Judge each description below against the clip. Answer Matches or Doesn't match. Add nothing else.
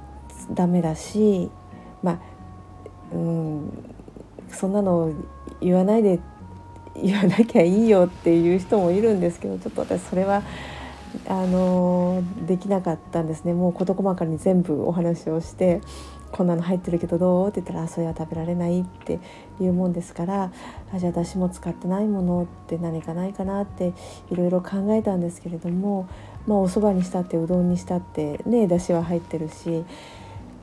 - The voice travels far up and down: Doesn't match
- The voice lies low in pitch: Doesn't match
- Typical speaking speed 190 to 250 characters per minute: Doesn't match